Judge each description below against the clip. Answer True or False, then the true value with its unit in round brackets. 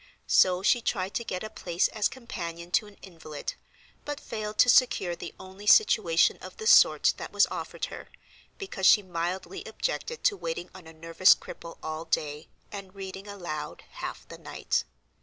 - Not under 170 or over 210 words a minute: True (175 wpm)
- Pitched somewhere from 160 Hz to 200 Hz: True (185 Hz)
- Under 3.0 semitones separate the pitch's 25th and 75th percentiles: False (4.0 semitones)